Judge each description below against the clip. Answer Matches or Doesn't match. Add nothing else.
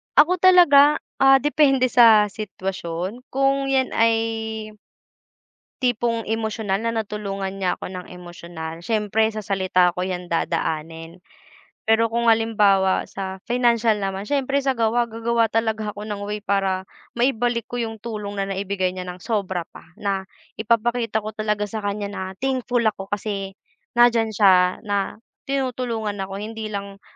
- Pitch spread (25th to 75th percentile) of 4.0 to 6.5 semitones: Doesn't match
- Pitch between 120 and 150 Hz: Doesn't match